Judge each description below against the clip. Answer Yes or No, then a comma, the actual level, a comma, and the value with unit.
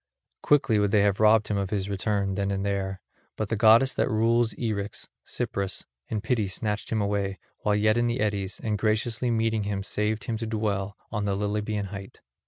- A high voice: No, low, 105 Hz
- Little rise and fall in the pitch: Yes, narrow, 1.8 semitones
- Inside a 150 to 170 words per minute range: No, average, 195 wpm